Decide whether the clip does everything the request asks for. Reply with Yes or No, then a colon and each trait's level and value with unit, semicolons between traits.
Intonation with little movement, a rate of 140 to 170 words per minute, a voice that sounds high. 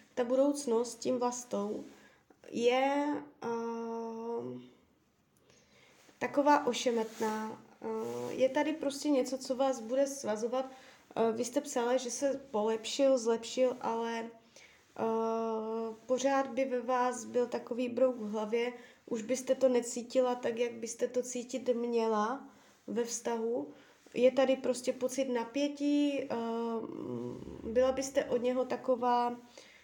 No: narrow, 2.2 semitones; average, 120 wpm; high, 245 Hz